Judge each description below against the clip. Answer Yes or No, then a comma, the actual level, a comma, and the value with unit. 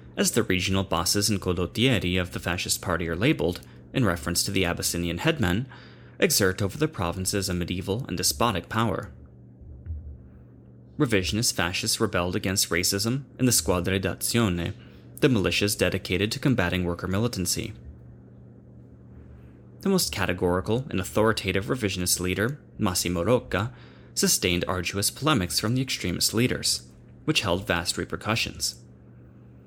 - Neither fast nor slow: No, slow, 125 wpm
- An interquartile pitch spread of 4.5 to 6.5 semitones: Yes, wide, 5.6 semitones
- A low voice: Yes, very low, 90 Hz